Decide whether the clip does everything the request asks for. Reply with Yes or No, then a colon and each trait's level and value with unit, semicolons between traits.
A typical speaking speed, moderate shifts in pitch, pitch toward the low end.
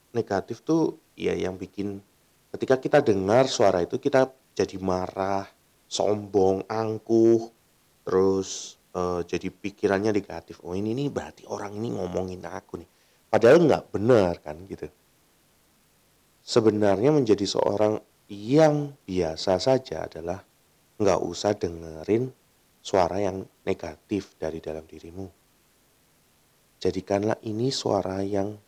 Yes: average, 115 wpm; average, 3.3 semitones; low, 100 Hz